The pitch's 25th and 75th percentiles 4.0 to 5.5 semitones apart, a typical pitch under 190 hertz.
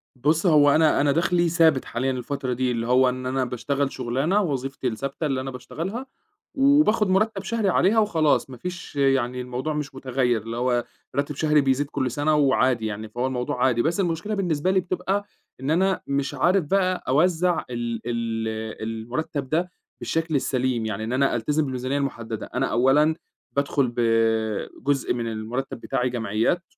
Yes: average, 4.7 semitones; low, 135 Hz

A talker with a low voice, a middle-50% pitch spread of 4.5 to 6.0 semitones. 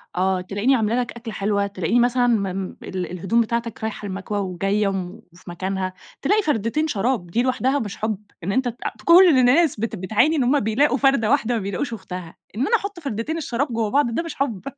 No: high, 225 Hz; average, 5.1 semitones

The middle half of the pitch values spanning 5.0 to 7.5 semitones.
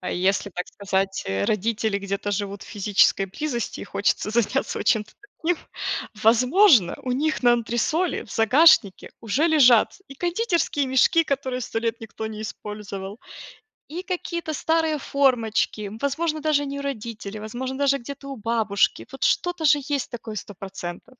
Yes: wide, 5.6 semitones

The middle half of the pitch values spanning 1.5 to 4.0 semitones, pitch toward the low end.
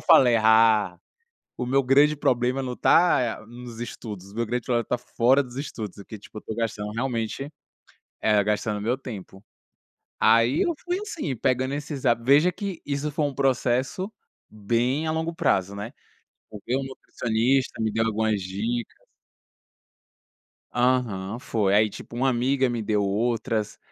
Yes: average, 3.7 semitones; low, 120 Hz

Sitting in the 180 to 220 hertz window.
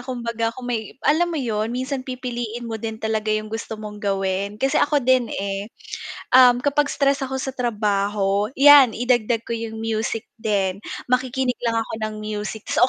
No: high, 230 Hz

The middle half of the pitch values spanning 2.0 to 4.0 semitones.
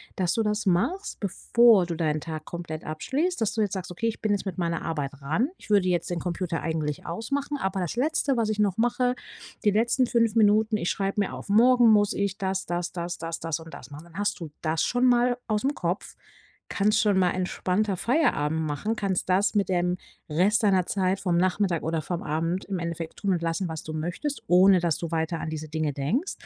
No: average, 4.5 semitones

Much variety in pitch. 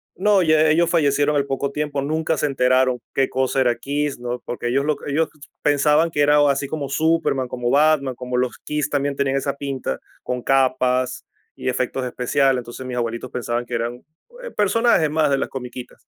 No: average, 2.8 semitones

